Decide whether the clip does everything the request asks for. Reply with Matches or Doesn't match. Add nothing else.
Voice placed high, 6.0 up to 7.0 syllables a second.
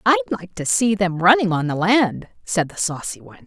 Doesn't match